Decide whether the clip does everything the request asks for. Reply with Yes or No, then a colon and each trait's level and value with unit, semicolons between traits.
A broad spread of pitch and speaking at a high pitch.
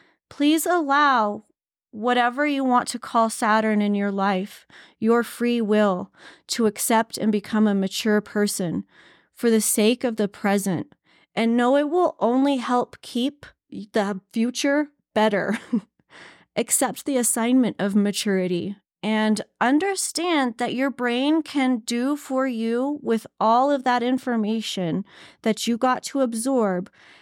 No: average, 3.8 semitones; high, 230 Hz